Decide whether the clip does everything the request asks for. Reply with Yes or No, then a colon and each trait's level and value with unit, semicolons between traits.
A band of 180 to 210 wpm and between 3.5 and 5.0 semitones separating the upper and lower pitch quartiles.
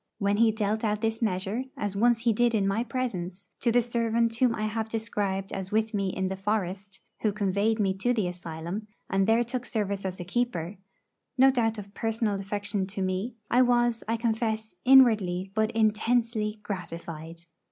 No: average, 185 wpm; average, 2.9 semitones